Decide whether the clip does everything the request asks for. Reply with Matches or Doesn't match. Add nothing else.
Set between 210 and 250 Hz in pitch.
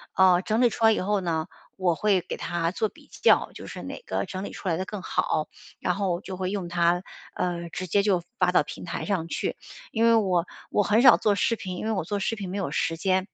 Doesn't match